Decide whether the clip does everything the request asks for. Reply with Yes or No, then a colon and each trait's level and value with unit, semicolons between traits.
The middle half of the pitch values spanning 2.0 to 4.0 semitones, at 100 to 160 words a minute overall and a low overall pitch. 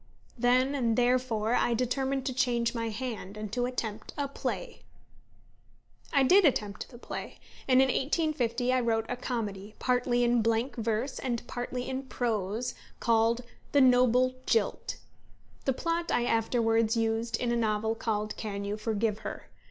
No: narrow, 2.4 semitones; average, 155 wpm; high, 240 Hz